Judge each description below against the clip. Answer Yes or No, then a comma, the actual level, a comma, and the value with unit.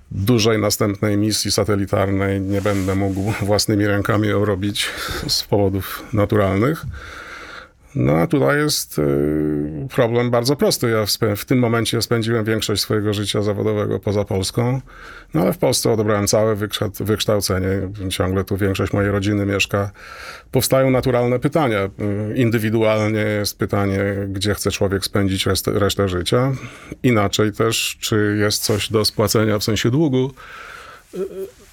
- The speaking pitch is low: Yes, low, 105 Hz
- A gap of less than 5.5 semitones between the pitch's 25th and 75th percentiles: Yes, narrow, 2.5 semitones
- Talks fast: No, average, 135 wpm